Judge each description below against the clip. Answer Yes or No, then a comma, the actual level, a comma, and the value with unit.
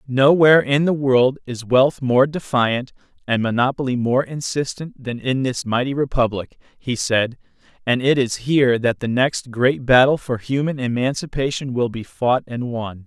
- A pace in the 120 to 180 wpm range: Yes, average, 165 wpm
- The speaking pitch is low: Yes, low, 130 Hz